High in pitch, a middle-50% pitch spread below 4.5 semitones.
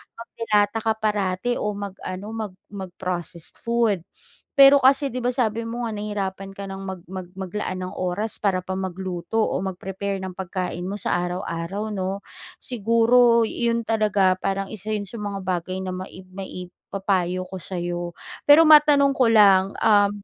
Yes: high, 195 Hz; average, 3.2 semitones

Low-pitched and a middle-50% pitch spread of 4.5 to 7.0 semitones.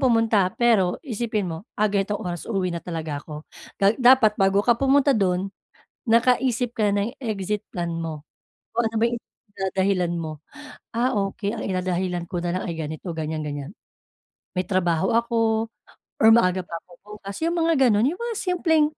No: high, 200 Hz; average, 4.8 semitones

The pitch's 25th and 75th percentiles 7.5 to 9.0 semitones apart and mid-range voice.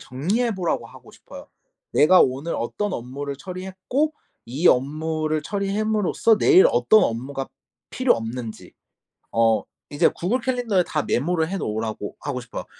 Yes: wide, 8.3 semitones; medium, 160 Hz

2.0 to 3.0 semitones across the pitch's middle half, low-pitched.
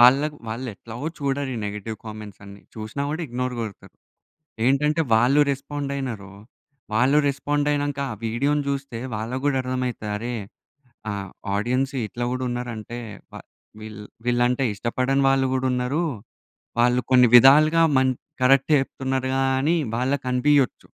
Yes: average, 2.7 semitones; low, 130 Hz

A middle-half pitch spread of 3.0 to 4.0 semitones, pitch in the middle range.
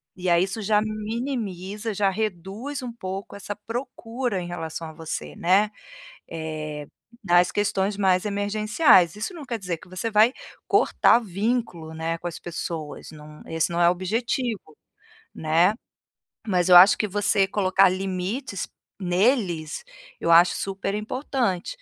No: average, 3.6 semitones; high, 195 Hz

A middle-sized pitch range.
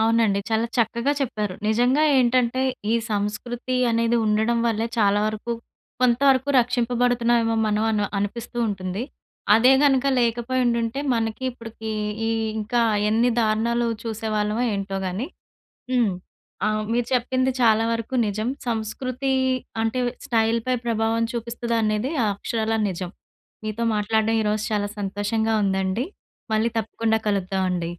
No: narrow, 2.0 semitones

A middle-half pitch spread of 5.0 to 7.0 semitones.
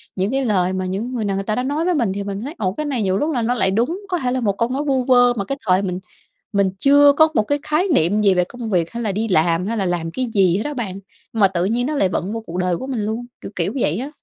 Yes: average, 5.3 semitones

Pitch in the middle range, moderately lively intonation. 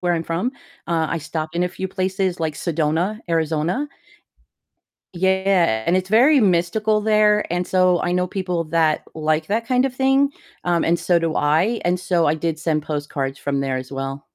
Yes: medium, 175 Hz; average, 3.4 semitones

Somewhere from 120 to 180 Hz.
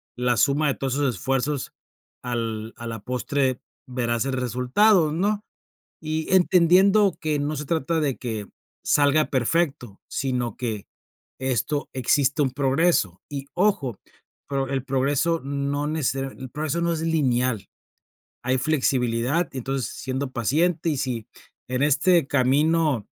Yes: low, 135 Hz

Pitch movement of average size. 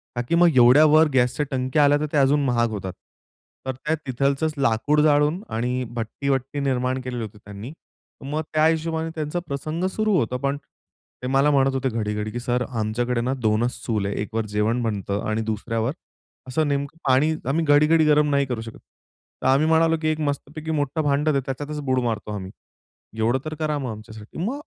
Yes: average, 4.2 semitones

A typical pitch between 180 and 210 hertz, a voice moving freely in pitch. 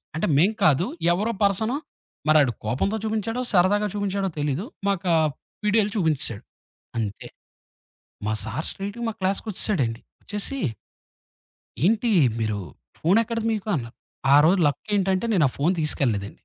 Yes: high, 190 Hz; wide, 6.4 semitones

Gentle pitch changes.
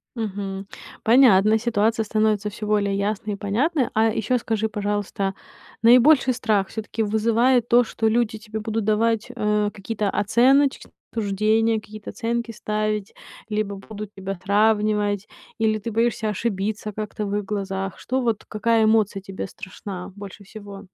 Yes: narrow, 1.9 semitones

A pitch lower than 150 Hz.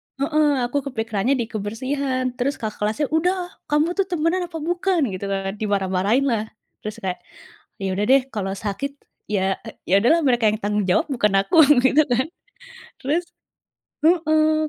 No: very high, 255 Hz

